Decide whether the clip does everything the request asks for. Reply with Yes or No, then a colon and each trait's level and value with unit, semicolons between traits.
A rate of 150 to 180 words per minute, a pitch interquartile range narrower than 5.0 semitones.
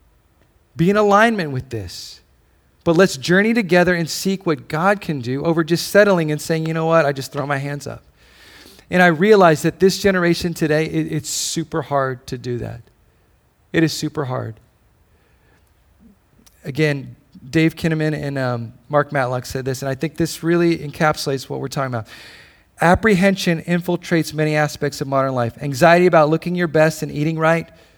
Yes: average, 175 wpm; average, 4.2 semitones